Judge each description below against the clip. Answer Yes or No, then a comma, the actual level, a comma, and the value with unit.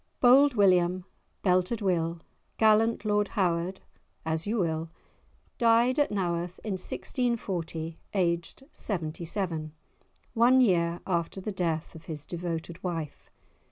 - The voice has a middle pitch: Yes, medium, 180 Hz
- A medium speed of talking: No, slow, 120 wpm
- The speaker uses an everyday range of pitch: Yes, average, 4.1 semitones